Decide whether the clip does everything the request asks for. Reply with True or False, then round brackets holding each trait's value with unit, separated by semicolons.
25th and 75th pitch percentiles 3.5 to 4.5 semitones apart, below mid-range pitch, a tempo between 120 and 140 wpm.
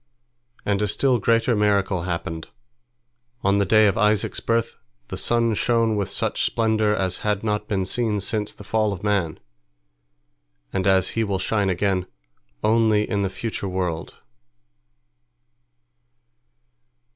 False (2.4 semitones; 105 Hz; 135 wpm)